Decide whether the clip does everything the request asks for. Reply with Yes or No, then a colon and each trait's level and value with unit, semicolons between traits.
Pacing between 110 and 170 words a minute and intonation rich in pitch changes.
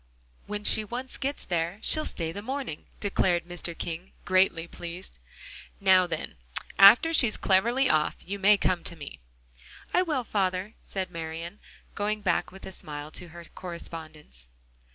No: average, 155 wpm; average, 3.8 semitones